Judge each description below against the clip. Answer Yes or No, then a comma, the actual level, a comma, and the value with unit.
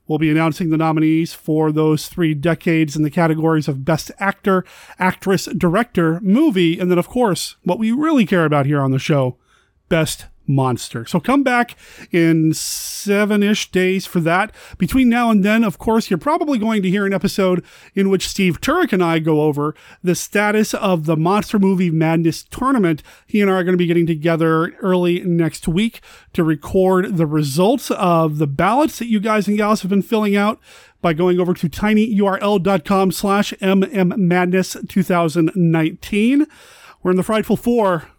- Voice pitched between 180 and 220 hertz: Yes, medium, 185 Hz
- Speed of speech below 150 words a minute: No, average, 175 wpm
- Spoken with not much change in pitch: No, average, 4.0 semitones